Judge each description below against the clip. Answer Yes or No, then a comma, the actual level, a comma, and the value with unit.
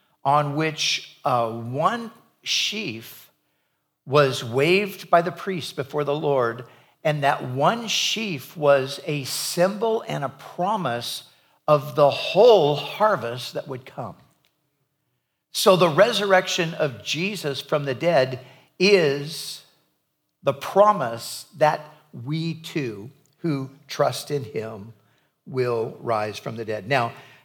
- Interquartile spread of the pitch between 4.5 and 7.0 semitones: Yes, average, 5.0 semitones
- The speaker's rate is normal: No, slow, 120 wpm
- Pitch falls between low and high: Yes, medium, 145 Hz